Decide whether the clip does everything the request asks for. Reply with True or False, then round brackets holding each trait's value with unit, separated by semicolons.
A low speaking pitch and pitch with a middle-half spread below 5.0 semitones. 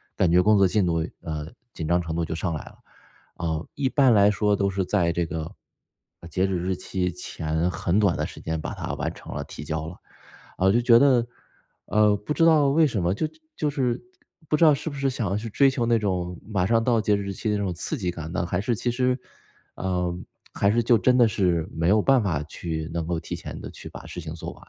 False (100 Hz; 5.6 semitones)